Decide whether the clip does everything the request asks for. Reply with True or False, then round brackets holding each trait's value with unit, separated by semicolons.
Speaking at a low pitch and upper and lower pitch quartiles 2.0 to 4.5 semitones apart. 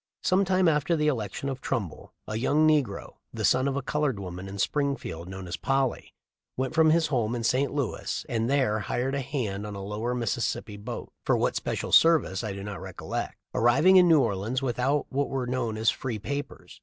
False (125 Hz; 5.1 semitones)